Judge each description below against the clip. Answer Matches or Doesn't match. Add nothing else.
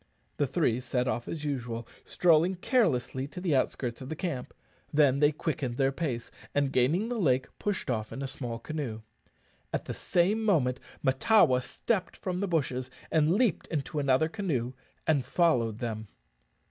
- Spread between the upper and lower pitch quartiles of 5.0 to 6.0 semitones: Matches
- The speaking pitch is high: Doesn't match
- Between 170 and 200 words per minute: Doesn't match